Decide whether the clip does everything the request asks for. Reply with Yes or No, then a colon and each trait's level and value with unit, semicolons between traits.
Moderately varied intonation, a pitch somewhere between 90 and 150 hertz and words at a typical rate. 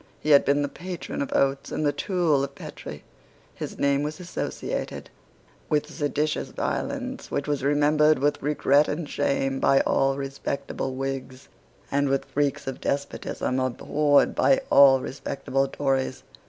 No: narrow, 1.8 semitones; medium, 140 Hz; average, 145 wpm